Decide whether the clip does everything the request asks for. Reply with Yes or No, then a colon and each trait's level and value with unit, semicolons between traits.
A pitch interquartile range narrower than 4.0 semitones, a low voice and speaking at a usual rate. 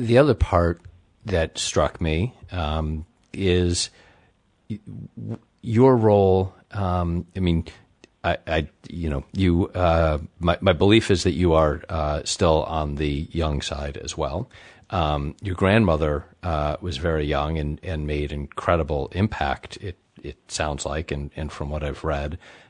Yes: average, 3.5 semitones; very low, 85 Hz; average, 150 wpm